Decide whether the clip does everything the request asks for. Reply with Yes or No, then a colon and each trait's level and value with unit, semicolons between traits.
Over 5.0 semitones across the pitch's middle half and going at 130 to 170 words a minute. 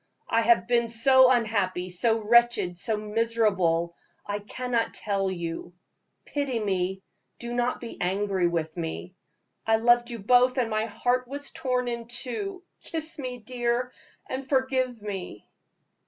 No: average, 4.3 semitones; average, 140 wpm